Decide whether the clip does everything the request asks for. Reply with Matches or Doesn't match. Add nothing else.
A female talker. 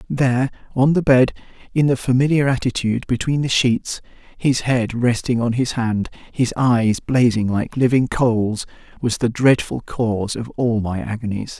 Doesn't match